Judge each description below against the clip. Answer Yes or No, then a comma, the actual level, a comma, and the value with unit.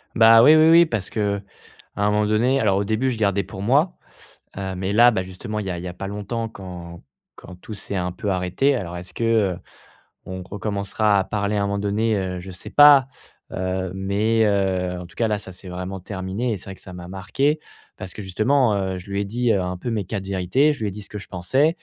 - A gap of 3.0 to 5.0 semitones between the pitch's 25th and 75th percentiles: Yes, average, 3.3 semitones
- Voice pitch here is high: No, low, 100 Hz